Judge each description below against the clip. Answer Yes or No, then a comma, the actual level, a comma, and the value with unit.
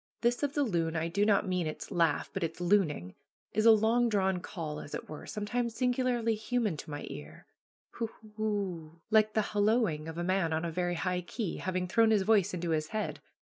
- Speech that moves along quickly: Yes, fast, 210 wpm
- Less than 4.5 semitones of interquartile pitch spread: No, average, 4.8 semitones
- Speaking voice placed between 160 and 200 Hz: Yes, high, 190 Hz